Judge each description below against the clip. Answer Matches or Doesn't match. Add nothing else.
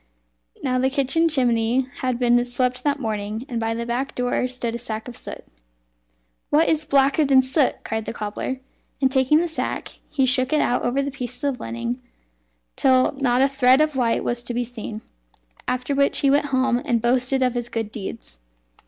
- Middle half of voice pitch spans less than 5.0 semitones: Matches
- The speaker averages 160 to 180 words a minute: Doesn't match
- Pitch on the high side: Matches